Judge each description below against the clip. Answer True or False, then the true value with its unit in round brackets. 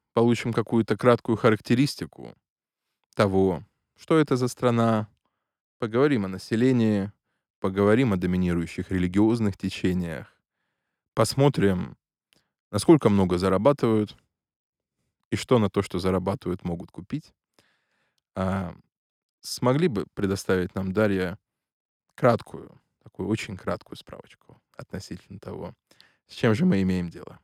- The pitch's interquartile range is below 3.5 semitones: False (3.8 semitones)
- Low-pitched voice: True (100 Hz)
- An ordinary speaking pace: False (105 wpm)